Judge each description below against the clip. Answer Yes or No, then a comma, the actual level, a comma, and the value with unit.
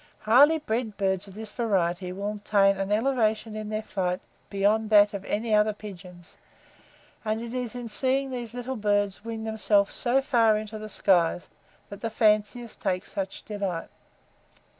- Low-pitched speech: No, high, 215 Hz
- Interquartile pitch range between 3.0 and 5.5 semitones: No, narrow, 2.4 semitones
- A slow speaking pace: No, average, 160 wpm